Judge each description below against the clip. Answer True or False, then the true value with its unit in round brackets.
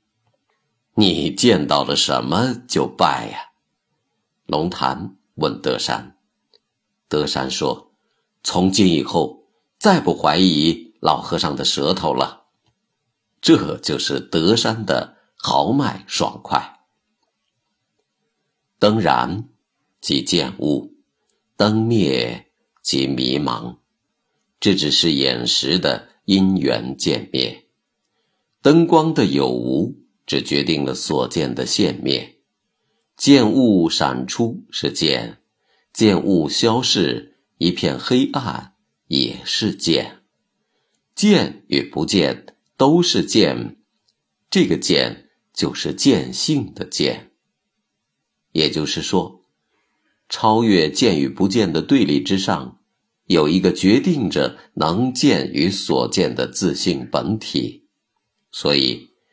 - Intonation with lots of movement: True (9.0 semitones)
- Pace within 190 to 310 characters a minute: False (145 characters per minute)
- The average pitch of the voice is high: False (95 Hz)